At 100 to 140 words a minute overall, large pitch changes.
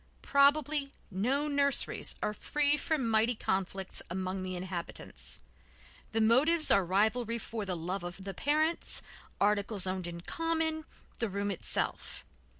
Yes: slow, 135 wpm; wide, 7.1 semitones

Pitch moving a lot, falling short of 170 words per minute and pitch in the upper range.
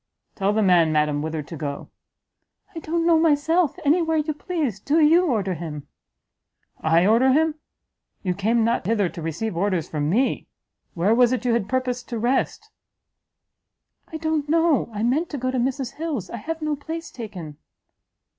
No: wide, 8.7 semitones; average, 175 wpm; high, 240 Hz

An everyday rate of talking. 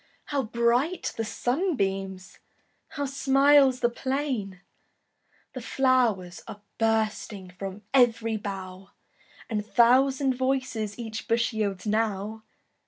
No: slow, 105 wpm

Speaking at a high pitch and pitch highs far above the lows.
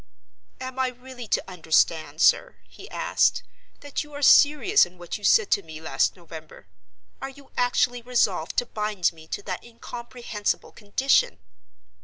Yes: high, 235 Hz; wide, 6.4 semitones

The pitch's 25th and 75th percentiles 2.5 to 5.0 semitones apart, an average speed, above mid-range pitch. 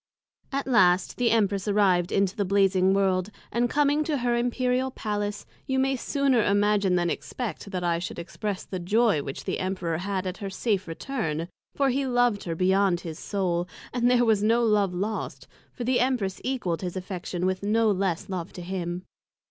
Yes: average, 4.6 semitones; average, 185 wpm; high, 200 Hz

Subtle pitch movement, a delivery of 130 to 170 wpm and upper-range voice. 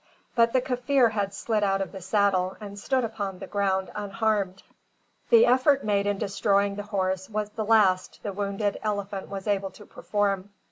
No: narrow, 2.0 semitones; average, 180 wpm; high, 205 Hz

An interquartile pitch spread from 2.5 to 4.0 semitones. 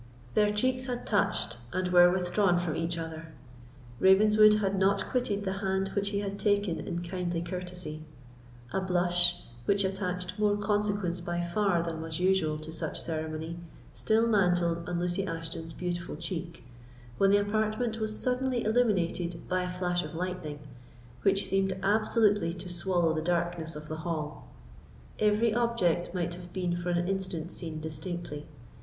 Yes: average, 3.0 semitones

